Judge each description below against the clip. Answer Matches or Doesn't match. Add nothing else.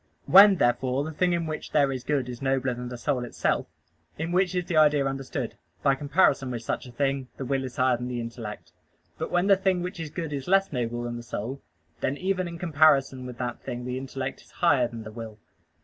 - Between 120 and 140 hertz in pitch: Matches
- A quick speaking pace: Matches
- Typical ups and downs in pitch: Matches